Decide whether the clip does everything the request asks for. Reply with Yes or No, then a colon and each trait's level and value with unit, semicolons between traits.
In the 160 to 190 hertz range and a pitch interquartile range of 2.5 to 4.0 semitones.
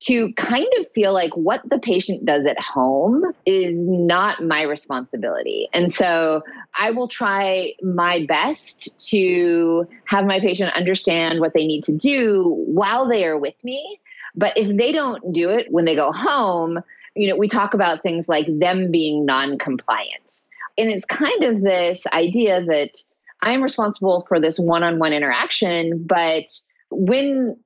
No: medium, 185 Hz; average, 5.0 semitones